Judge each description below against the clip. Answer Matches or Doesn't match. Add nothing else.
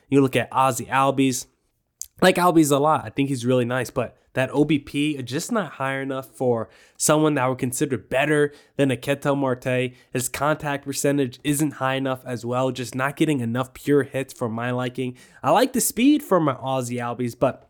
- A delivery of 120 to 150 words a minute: Doesn't match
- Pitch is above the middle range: Doesn't match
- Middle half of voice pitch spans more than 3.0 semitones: Doesn't match